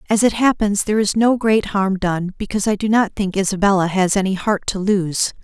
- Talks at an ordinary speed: No, fast, 220 wpm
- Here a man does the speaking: No, female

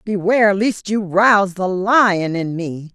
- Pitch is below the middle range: No, high, 195 Hz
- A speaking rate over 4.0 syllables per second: No, 3.9 syllables/s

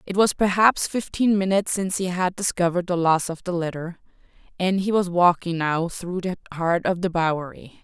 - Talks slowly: No, average, 190 wpm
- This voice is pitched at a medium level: Yes, medium, 180 Hz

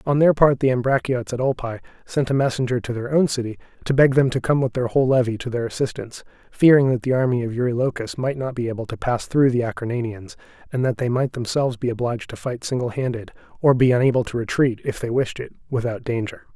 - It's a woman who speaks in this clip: No, male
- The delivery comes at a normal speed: No, fast, 230 wpm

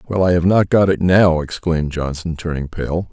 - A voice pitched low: Yes, very low, 85 Hz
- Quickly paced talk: Yes, fast, 210 wpm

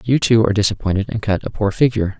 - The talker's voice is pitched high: No, low, 110 Hz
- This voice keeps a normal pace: No, fast, 245 wpm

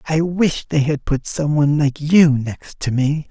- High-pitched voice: No, medium, 150 Hz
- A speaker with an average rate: No, fast, 220 wpm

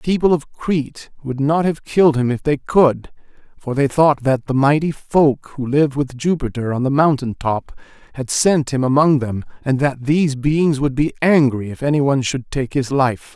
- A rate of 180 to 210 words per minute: Yes, fast, 205 wpm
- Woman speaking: No, male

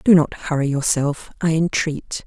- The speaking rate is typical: Yes, average, 160 wpm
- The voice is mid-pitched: Yes, medium, 155 Hz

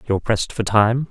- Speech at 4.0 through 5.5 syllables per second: No, 6.2 syllables/s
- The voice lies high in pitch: No, low, 110 Hz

